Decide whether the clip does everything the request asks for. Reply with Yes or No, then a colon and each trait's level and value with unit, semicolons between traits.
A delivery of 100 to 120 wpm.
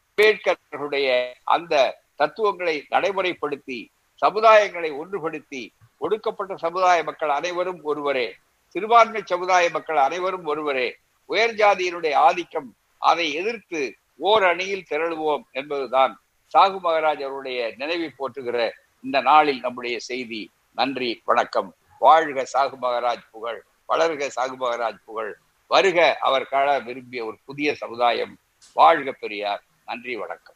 Yes: average, 105 wpm